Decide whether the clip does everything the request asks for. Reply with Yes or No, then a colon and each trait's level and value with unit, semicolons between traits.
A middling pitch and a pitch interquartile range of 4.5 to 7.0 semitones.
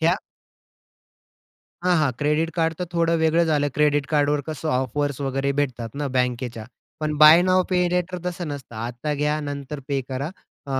No: medium, 150 Hz; average, 3.1 semitones